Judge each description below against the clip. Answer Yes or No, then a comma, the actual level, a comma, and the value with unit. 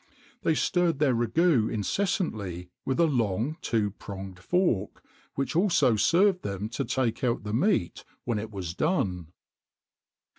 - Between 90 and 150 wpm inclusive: Yes, average, 140 wpm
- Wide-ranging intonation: Yes, wide, 8.4 semitones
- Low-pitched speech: Yes, low, 120 Hz